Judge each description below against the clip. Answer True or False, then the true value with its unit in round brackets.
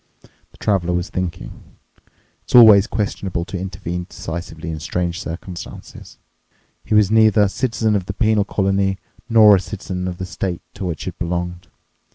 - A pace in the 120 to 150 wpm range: False (160 wpm)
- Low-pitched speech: True (95 Hz)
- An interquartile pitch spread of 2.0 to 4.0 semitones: True (2.9 semitones)